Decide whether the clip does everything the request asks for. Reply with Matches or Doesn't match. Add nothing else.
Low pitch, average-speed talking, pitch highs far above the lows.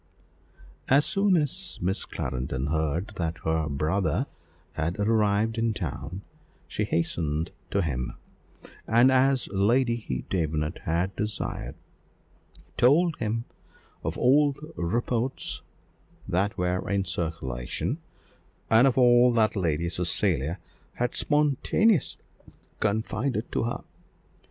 Doesn't match